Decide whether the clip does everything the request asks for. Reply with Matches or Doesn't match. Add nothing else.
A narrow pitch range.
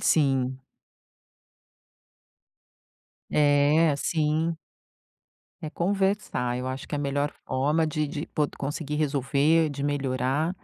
Matches